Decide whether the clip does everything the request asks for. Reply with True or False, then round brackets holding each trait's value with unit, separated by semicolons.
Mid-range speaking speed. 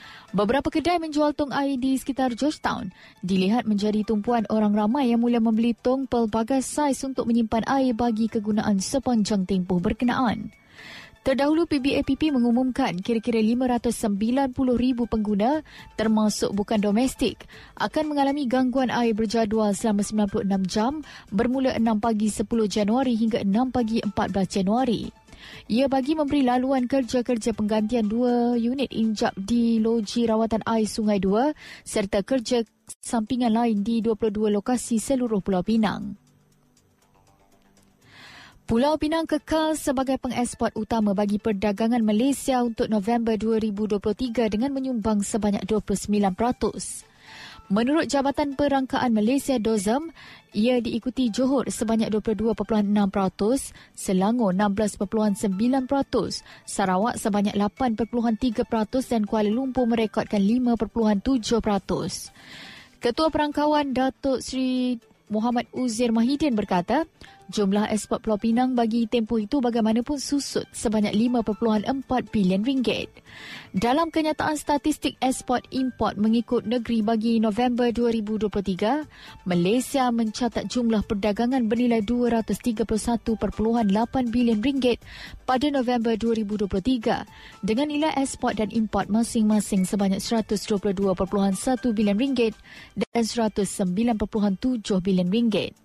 True (105 wpm)